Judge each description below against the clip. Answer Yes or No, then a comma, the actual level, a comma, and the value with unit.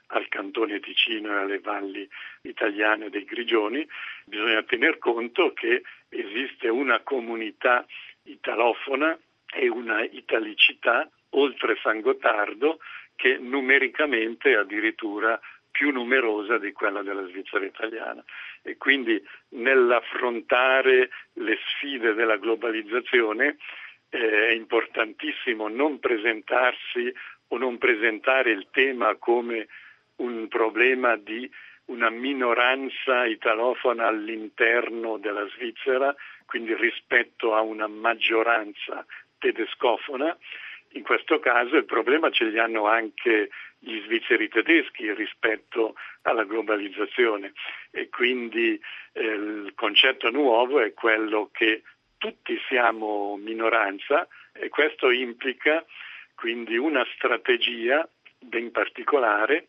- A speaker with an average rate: No, slow, 105 wpm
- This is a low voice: Yes, low, 130 Hz